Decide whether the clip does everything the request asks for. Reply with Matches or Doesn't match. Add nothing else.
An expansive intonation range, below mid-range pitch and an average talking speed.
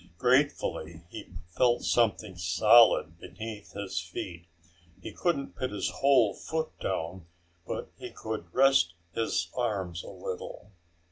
Doesn't match